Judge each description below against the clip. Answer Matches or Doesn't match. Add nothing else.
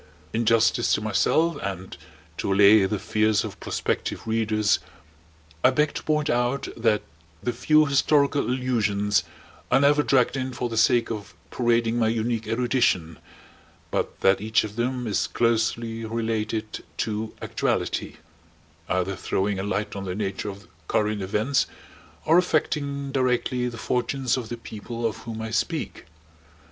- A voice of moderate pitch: Doesn't match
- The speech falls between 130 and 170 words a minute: Matches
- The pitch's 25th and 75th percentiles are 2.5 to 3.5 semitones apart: Matches